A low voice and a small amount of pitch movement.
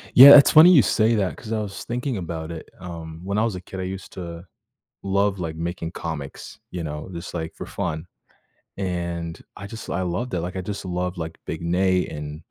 No: very low, 90 Hz; average, 3.1 semitones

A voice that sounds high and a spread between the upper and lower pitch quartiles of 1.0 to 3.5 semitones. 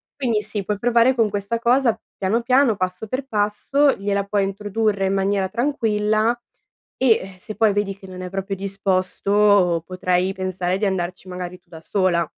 Yes: high, 200 Hz; average, 2.9 semitones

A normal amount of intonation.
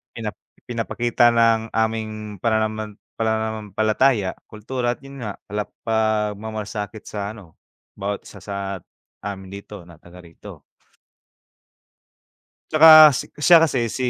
No: narrow, 2.1 semitones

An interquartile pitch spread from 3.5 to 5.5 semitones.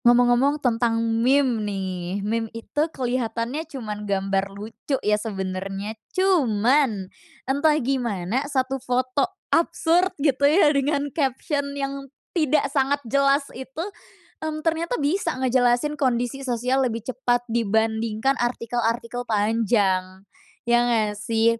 Yes: average, 4.0 semitones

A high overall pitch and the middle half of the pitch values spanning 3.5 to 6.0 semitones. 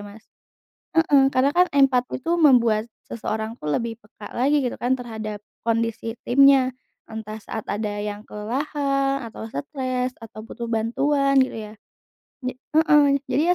Yes: high, 245 Hz; average, 4.0 semitones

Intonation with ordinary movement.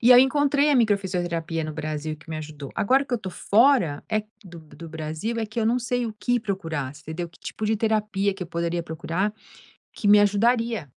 No: wide, 6.0 semitones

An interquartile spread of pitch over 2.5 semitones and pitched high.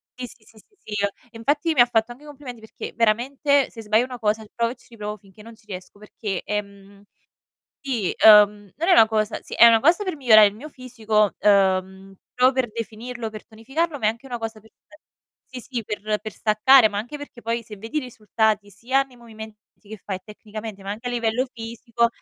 Yes: average, 2.9 semitones; high, 225 Hz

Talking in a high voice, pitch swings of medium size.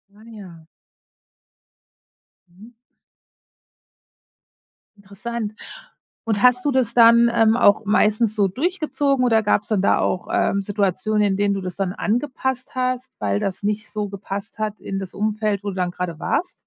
Yes: high, 210 Hz; average, 3.2 semitones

